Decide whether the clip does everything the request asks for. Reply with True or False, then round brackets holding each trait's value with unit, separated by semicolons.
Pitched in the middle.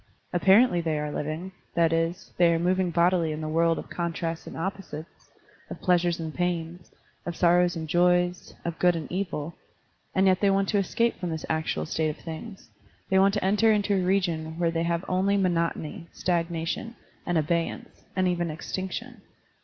True (175 Hz)